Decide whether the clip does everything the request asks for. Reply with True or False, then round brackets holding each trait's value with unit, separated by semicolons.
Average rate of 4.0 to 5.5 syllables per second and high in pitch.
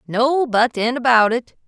True (4.1 syllables/s; 240 Hz)